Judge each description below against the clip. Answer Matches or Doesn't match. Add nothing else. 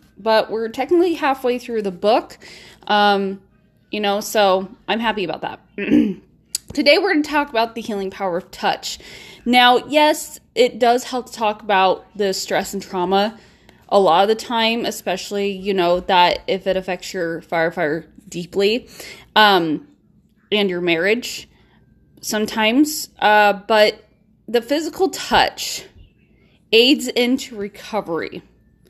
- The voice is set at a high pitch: Matches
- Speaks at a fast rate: Doesn't match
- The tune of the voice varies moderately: Matches